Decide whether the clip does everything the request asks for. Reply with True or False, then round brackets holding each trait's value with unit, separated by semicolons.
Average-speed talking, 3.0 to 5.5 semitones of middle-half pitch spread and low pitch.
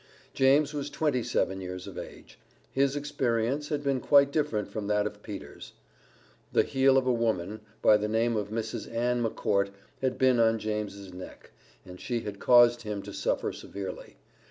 True (175 wpm; 4.3 semitones; 115 Hz)